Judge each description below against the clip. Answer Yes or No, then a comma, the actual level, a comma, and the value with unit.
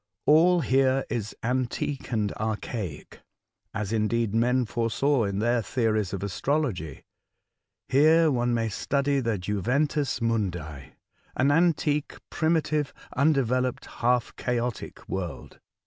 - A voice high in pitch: No, low, 120 Hz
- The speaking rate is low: Yes, slow, 115 wpm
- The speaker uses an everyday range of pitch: Yes, average, 4.6 semitones